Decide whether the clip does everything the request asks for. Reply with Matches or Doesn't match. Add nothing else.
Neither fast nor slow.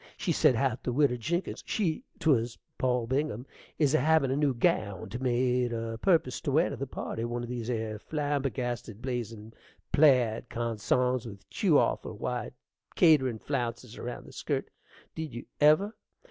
Matches